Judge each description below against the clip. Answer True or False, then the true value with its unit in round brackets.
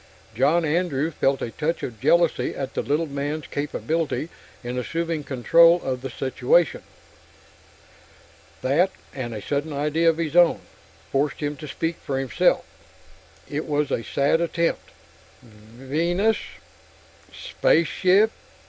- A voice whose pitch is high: False (150 Hz)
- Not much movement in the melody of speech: False (3.7 semitones)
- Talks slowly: True (125 wpm)